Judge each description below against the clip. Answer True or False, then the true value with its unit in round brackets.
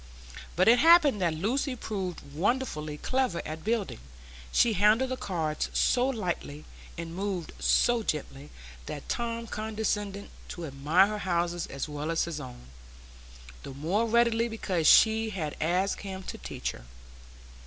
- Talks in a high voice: True (195 Hz)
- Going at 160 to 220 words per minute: False (145 wpm)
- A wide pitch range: True (6.1 semitones)